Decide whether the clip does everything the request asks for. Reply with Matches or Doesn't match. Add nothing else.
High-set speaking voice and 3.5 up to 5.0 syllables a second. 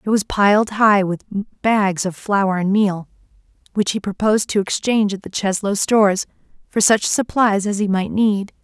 Matches